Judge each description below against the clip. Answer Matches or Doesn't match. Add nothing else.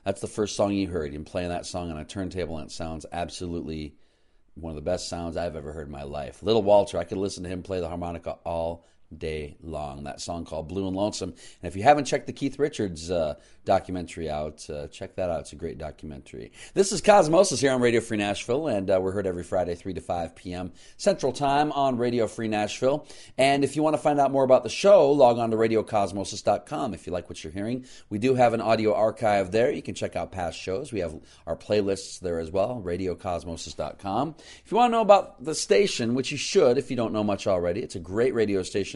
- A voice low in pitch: Matches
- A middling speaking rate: Doesn't match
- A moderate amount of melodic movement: Doesn't match